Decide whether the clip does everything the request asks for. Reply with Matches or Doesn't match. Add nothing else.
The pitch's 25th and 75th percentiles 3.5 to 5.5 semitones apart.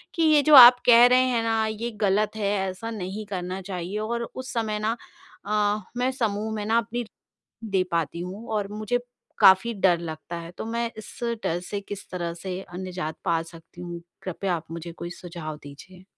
Matches